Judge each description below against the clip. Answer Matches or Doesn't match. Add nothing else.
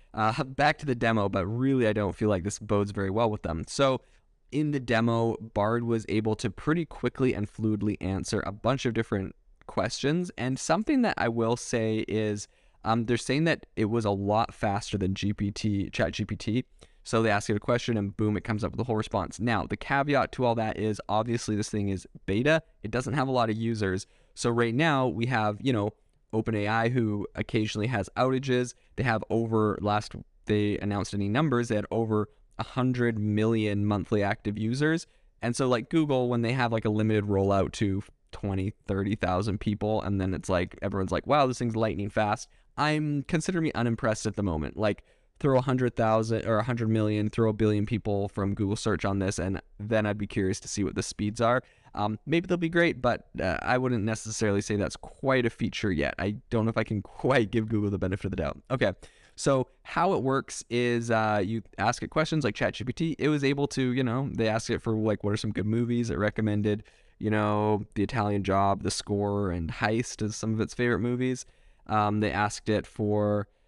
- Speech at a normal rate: Doesn't match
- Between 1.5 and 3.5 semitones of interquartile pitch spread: Matches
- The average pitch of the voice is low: Matches